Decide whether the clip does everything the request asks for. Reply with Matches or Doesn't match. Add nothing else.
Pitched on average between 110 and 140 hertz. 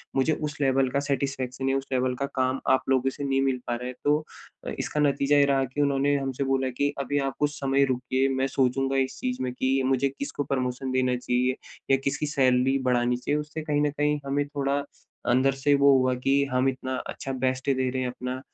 Matches